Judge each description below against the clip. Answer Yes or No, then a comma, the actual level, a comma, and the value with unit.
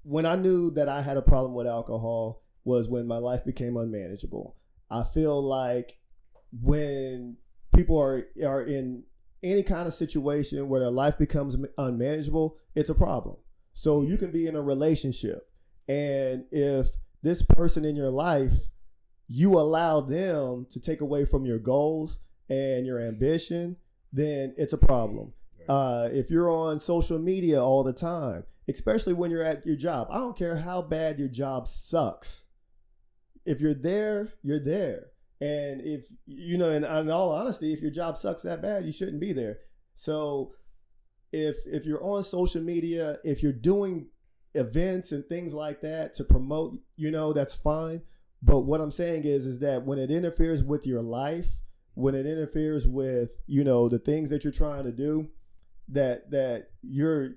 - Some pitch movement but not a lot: Yes, average, 3.7 semitones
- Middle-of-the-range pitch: Yes, medium, 145 Hz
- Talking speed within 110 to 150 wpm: No, average, 170 wpm